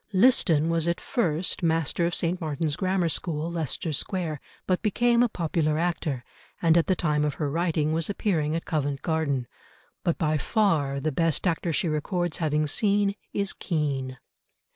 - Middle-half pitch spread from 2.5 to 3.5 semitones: Yes, average, 2.9 semitones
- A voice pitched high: No, medium, 165 Hz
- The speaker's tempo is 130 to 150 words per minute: No, average, 165 wpm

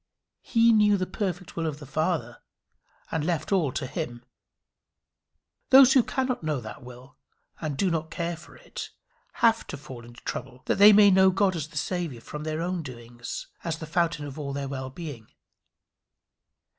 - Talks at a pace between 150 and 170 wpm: No, average, 180 wpm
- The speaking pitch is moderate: Yes, medium, 160 Hz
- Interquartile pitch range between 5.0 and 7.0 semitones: Yes, wide, 5.4 semitones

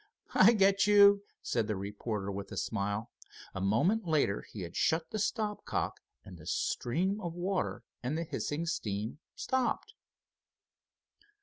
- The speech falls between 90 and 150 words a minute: Yes, average, 145 wpm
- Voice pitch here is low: No, medium, 155 Hz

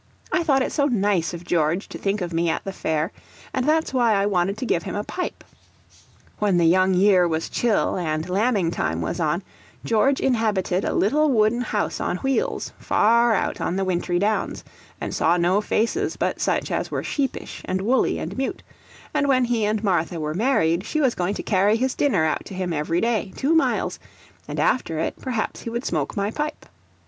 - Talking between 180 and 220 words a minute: Yes, fast, 205 wpm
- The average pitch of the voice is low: No, high, 205 Hz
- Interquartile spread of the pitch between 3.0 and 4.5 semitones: No, wide, 5.5 semitones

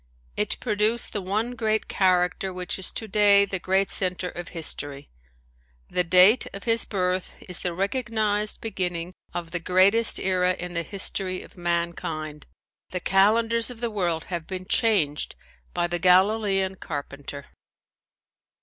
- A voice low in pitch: No, medium, 185 Hz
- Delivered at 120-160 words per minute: Yes, average, 140 wpm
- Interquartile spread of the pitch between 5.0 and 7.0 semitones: No, average, 3.2 semitones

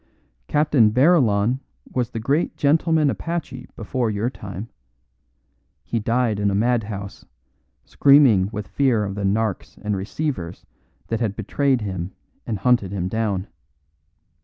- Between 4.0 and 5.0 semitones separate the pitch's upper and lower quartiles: Yes, average, 4.5 semitones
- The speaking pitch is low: Yes, low, 110 Hz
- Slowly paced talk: Yes, slow, 130 wpm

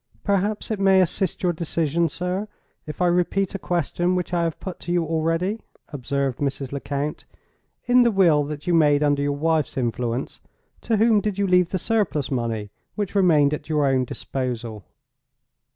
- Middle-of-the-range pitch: Yes, medium, 165 Hz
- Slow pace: No, average, 175 wpm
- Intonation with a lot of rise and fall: No, average, 4.8 semitones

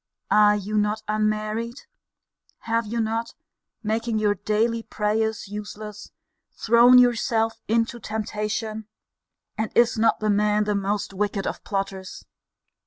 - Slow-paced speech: Yes, slow, 120 wpm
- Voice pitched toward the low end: No, high, 215 Hz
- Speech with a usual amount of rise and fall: No, narrow, 1.4 semitones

